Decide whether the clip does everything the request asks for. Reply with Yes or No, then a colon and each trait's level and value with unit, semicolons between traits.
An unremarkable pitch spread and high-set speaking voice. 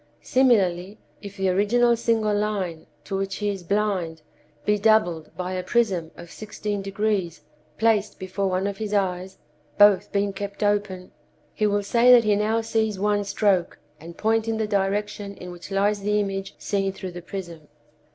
No: narrow, 2.1 semitones; high, 200 Hz